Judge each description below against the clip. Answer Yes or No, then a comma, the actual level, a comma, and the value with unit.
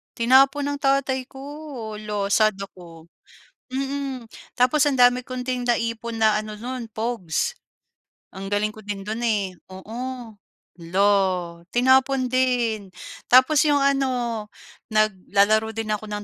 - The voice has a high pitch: Yes, high, 230 Hz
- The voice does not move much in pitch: No, average, 3.7 semitones